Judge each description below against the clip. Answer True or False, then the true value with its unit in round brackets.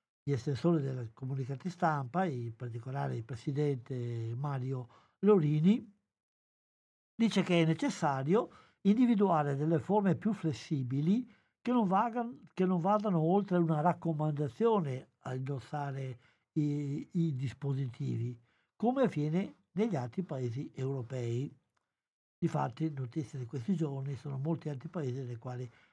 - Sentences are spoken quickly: False (120 wpm)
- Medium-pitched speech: True (150 Hz)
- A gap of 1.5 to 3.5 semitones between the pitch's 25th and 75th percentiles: False (5.4 semitones)